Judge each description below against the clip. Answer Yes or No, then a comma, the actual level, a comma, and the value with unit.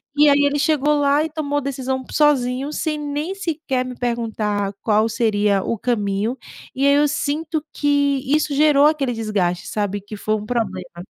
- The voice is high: Yes, very high, 265 Hz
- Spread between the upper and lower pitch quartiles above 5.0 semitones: Yes, wide, 5.4 semitones